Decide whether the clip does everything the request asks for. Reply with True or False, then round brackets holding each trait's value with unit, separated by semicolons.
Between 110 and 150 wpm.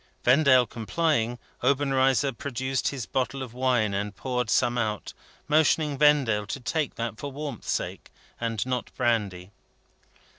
True (135 wpm)